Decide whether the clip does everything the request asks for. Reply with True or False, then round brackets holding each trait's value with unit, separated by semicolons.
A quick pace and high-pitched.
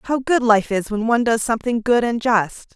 True (240 wpm; 230 Hz)